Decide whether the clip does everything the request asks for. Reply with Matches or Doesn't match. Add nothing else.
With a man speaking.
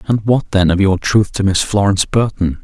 Matches